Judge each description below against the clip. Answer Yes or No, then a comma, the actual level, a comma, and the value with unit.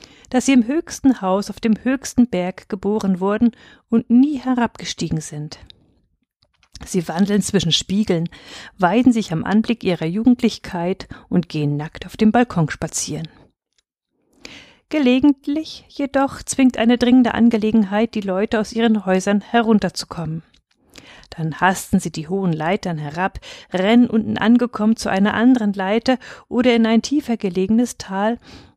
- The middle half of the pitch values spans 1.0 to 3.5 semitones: No, average, 4.5 semitones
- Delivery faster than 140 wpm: No, average, 135 wpm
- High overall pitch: Yes, high, 215 Hz